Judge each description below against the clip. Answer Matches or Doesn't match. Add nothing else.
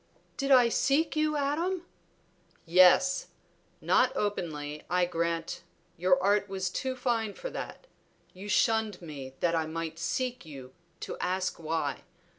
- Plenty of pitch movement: Matches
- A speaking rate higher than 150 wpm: Doesn't match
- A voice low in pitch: Doesn't match